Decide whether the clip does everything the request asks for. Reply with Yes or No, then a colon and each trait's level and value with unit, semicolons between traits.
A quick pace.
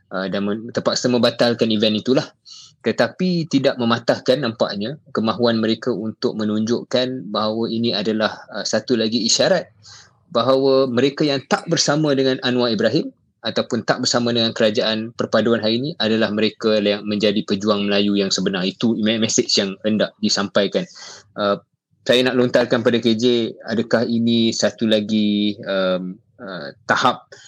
No: average, 140 wpm